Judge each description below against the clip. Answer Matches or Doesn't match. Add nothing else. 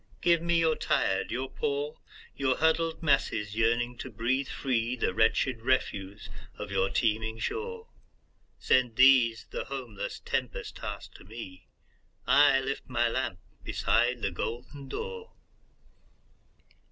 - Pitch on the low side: Matches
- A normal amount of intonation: Doesn't match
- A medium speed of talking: Doesn't match